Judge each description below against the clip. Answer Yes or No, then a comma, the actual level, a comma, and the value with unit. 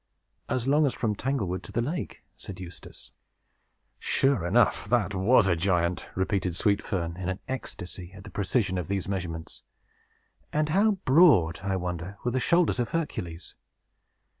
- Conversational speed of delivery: Yes, average, 160 wpm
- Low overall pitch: Yes, low, 100 Hz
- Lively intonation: Yes, wide, 6.1 semitones